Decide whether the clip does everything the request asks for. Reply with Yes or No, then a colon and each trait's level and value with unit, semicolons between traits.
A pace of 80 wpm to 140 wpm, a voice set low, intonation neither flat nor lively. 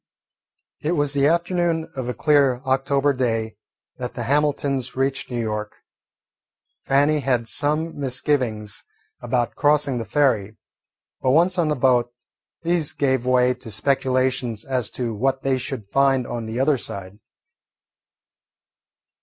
Yes: slow, 135 wpm; low, 130 Hz; average, 3.2 semitones